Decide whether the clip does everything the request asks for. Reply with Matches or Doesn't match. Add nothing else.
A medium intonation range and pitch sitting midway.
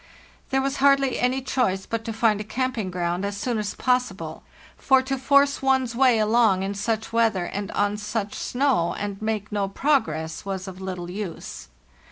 Doesn't match